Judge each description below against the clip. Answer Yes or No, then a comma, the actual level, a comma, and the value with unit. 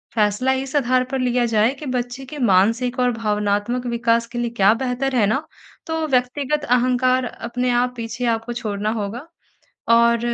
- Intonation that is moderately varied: No, narrow, 1.9 semitones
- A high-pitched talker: Yes, high, 245 Hz